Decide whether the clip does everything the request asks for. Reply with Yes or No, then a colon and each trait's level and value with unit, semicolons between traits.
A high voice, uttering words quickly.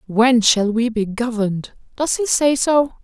No: high, 240 Hz; average, 180 wpm